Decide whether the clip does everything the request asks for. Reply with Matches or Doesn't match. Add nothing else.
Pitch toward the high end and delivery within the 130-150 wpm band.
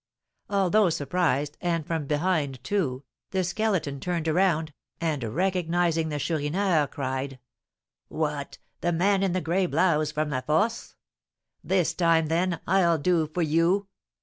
Doesn't match